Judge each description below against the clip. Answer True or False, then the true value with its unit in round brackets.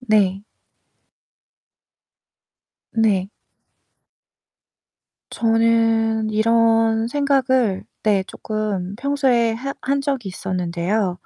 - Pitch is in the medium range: False (225 Hz)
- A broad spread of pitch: False (3.0 semitones)